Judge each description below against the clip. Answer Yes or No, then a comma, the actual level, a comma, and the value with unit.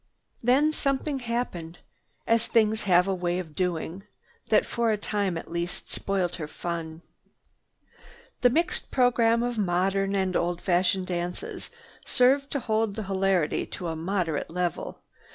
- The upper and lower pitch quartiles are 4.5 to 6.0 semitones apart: Yes, average, 4.8 semitones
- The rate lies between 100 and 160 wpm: Yes, average, 145 wpm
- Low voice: No, high, 195 Hz